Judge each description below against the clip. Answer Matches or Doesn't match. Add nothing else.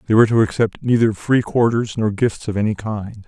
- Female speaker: Doesn't match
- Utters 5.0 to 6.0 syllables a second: Matches